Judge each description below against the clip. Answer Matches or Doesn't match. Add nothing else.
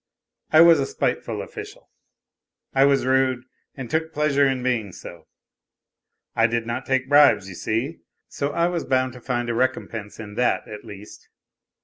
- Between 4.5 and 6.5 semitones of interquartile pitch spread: Doesn't match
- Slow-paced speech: Doesn't match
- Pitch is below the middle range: Matches